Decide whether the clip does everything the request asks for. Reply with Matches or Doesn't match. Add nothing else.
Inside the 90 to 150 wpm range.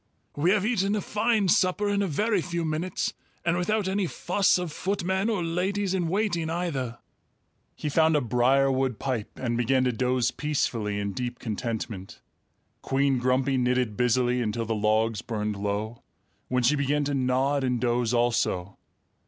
Doesn't match